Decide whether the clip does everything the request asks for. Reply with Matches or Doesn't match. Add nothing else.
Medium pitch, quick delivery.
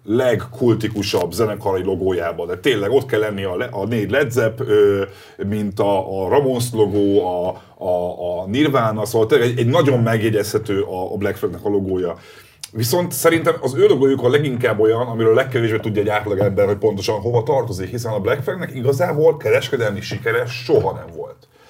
Doesn't match